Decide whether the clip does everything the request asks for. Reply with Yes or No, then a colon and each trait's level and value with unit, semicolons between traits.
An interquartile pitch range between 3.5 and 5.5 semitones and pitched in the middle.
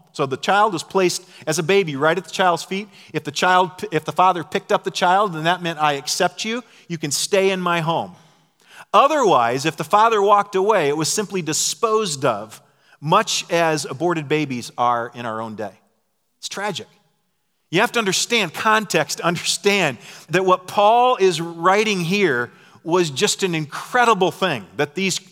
Yes: average, 4.0 semitones; medium, 180 Hz